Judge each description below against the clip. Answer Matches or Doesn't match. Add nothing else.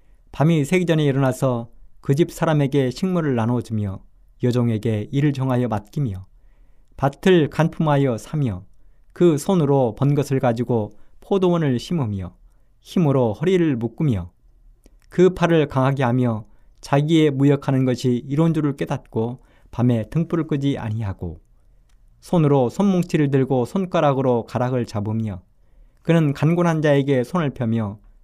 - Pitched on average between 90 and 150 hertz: Matches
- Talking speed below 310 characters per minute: Matches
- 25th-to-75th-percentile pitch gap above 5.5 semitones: Doesn't match